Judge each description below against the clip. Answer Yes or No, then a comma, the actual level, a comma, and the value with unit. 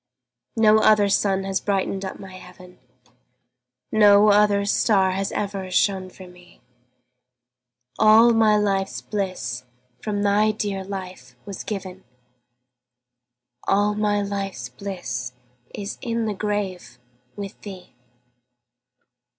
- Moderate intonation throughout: No, narrow, 1.9 semitones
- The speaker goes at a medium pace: No, slow, 110 wpm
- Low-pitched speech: No, high, 200 Hz